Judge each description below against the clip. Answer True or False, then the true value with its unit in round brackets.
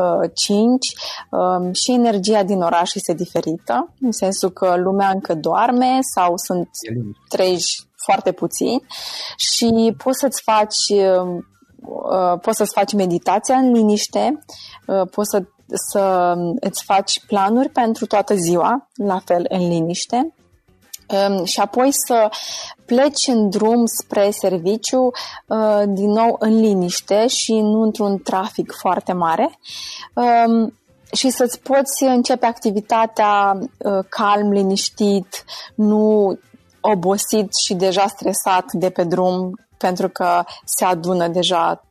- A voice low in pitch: False (205 Hz)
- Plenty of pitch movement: False (3.7 semitones)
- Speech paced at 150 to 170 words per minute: False (115 wpm)